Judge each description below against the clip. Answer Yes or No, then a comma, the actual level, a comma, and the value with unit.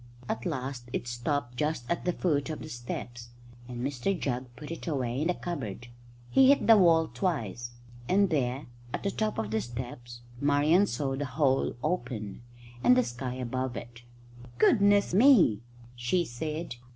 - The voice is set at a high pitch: No, low, 135 Hz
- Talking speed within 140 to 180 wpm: Yes, average, 165 wpm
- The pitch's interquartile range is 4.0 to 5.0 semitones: No, wide, 5.5 semitones